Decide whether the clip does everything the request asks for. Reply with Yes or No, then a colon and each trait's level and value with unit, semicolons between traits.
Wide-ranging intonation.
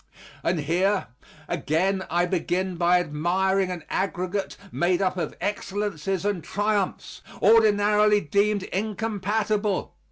No: narrow, 2.5 semitones